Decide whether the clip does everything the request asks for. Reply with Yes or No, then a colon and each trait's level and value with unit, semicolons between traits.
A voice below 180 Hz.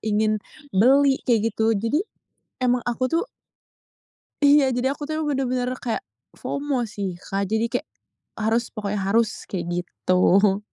No: high, 230 Hz